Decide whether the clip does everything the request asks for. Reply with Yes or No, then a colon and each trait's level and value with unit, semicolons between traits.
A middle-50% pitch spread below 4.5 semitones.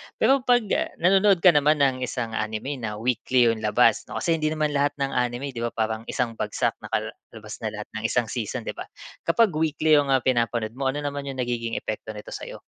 No: average, 4.9 semitones